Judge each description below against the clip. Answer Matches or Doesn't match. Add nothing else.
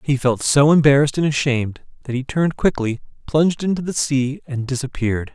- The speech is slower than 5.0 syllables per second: Doesn't match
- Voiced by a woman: Doesn't match